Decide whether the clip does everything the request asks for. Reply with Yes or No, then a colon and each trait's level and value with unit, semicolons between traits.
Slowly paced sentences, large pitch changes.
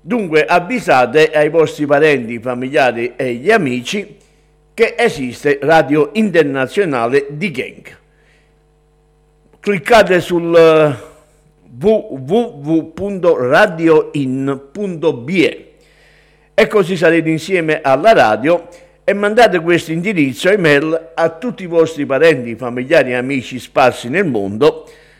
No: slow, 95 wpm; average, 4.2 semitones